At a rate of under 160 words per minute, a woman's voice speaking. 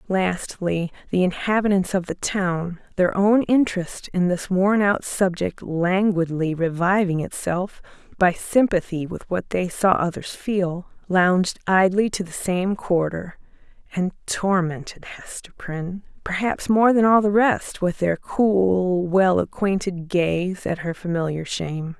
Yes: average, 140 wpm; female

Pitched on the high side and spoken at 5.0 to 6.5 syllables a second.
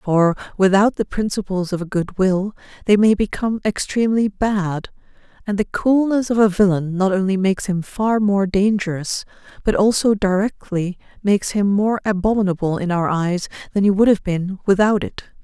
Yes: high, 195 Hz; 5.1 syllables/s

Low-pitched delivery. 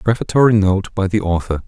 Yes: low, 100 Hz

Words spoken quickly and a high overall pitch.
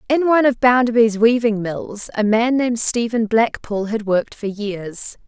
No: average, 170 wpm; high, 225 Hz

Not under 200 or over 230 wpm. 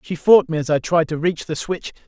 No: fast, 290 wpm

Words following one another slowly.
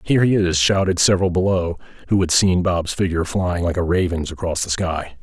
No: fast, 205 wpm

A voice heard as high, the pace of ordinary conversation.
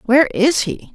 Yes: very high, 255 Hz; average, 190 wpm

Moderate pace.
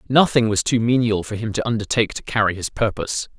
No: fast, 215 wpm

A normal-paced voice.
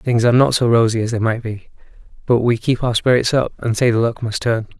No: fast, 265 wpm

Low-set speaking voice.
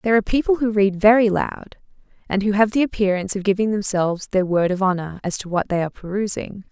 No: high, 200 Hz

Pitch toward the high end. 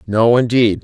No: low, 115 Hz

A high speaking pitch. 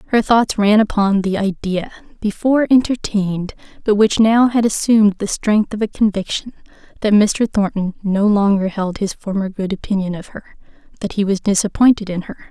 Yes: high, 205 Hz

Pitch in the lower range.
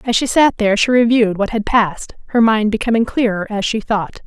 No: high, 220 Hz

